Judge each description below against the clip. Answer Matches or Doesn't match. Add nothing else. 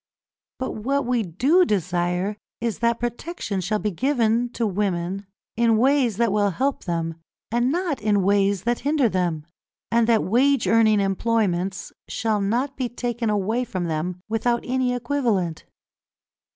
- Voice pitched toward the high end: Matches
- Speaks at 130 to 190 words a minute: Matches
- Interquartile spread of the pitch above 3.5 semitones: Matches